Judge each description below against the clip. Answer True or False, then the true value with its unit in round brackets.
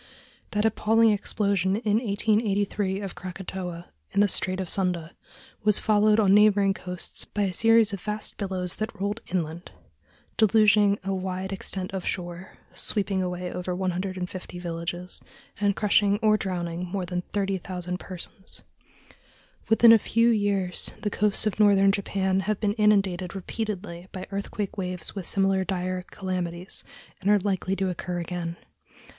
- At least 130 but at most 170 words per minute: True (150 wpm)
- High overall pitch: True (195 Hz)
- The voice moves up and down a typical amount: False (2.3 semitones)